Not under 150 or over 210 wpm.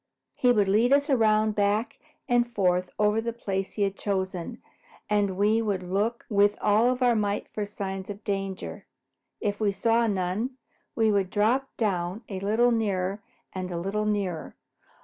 Yes: average, 170 wpm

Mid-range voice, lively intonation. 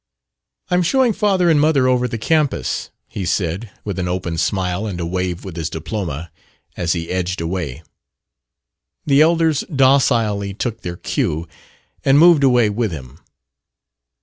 No: low, 100 Hz; wide, 8.0 semitones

